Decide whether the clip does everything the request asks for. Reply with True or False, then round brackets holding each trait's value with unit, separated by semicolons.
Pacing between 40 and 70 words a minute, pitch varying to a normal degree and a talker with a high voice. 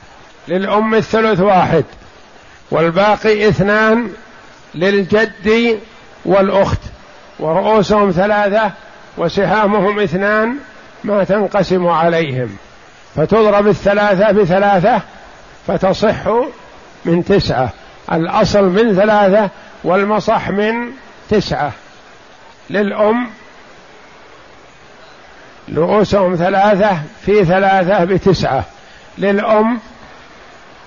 False (65 wpm; 2.1 semitones; 205 Hz)